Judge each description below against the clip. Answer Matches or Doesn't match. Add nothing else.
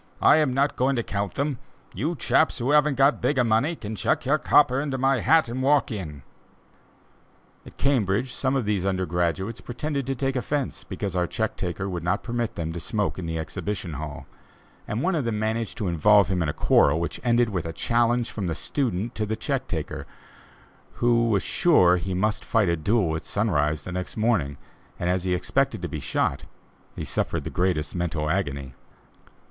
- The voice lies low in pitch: Matches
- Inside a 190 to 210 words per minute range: Matches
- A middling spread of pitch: Doesn't match